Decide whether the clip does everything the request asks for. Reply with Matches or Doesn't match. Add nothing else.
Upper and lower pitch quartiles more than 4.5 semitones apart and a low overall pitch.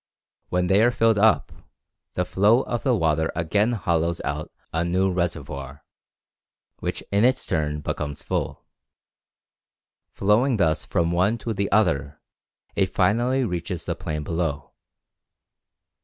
Matches